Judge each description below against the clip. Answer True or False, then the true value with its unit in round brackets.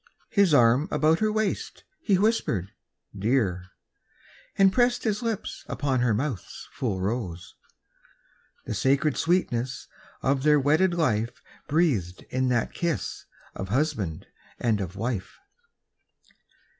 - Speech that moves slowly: True (120 wpm)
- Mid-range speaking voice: False (130 Hz)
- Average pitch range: False (8.1 semitones)